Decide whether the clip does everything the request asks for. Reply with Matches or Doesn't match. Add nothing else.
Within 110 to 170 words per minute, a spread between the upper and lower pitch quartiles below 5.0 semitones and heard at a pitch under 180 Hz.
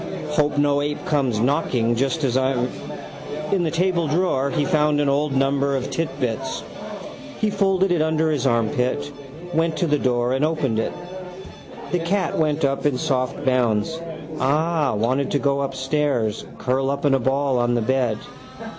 Matches